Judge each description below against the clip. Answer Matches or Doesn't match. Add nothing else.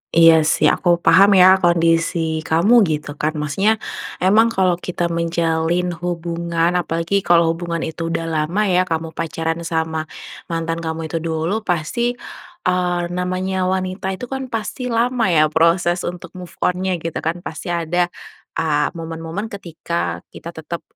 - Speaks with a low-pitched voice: Doesn't match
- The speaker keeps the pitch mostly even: Matches